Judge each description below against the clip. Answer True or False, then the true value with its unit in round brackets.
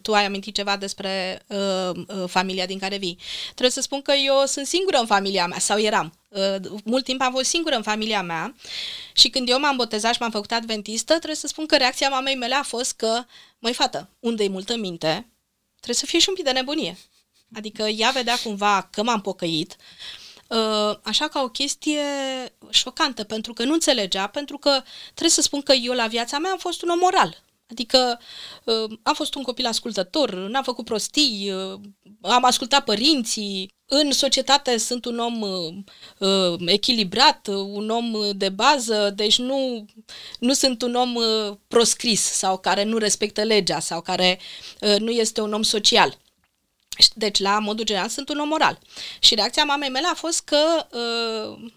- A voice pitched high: True (230 Hz)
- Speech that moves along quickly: True (175 wpm)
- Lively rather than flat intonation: False (5.0 semitones)